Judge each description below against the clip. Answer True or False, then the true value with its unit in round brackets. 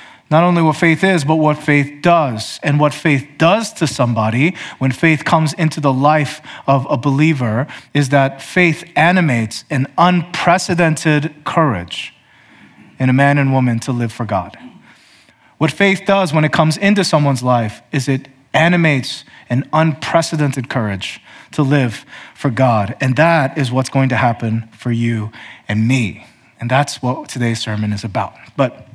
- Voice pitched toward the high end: False (140 Hz)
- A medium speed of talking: True (160 wpm)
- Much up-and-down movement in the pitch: False (4.3 semitones)